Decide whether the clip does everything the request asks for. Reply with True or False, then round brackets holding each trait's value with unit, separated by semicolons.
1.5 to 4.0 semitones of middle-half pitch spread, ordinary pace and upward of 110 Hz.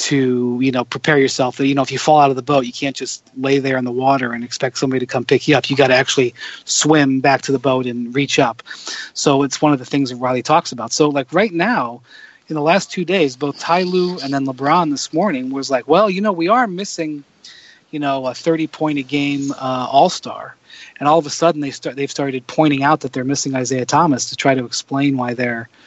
False (2.7 semitones; 250 wpm; 140 Hz)